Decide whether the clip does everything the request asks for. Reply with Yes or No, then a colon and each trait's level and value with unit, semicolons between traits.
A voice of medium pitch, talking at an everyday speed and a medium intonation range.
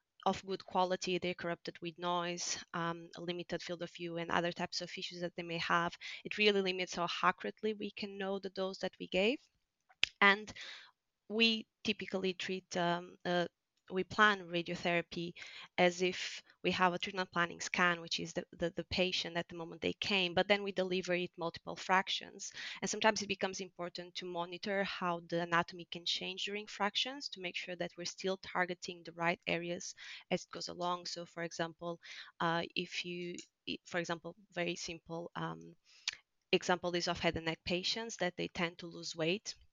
No: medium, 175 Hz; average, 185 wpm; narrow, 1.7 semitones